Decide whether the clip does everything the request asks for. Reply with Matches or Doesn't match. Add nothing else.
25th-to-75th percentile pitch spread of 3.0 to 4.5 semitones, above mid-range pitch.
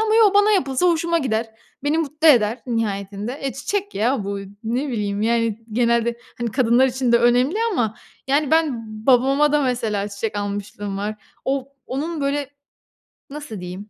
Doesn't match